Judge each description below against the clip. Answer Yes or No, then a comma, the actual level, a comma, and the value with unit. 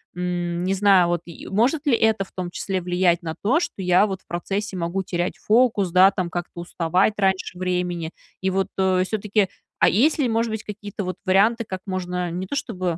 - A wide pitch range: No, average, 2.7 semitones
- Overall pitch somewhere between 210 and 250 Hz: No, high, 190 Hz